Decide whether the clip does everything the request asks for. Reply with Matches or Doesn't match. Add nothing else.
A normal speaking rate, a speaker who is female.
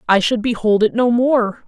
Doesn't match